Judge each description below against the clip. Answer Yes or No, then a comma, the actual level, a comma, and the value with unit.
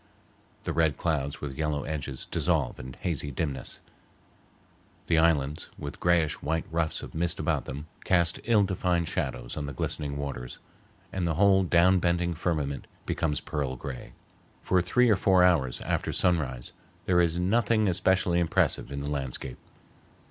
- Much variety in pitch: No, average, 3.8 semitones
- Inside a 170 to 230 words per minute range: No, average, 155 wpm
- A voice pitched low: Yes, very low, 80 Hz